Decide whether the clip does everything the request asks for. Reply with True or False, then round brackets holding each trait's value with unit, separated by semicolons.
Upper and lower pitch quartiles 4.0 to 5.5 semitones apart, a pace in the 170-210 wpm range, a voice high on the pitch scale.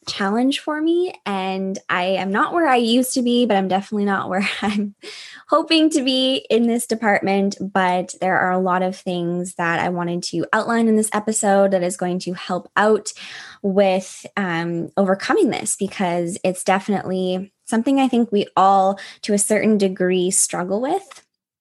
False (3.4 semitones; 175 wpm; 195 Hz)